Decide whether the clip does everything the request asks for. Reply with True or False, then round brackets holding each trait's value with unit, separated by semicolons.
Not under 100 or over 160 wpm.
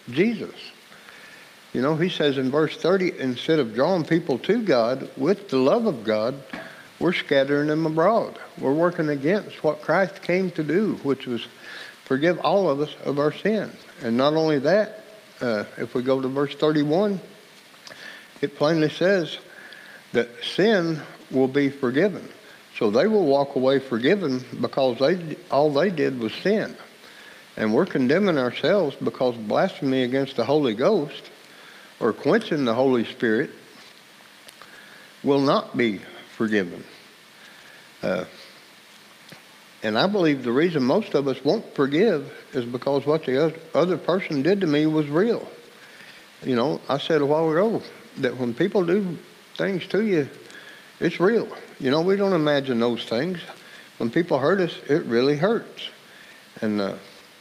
True (150 wpm)